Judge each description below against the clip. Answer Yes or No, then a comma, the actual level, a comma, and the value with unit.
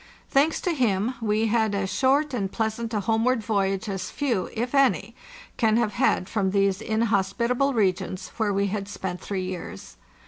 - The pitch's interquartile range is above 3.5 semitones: No, average, 3.2 semitones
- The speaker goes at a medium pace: Yes, average, 180 wpm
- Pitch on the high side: Yes, high, 215 Hz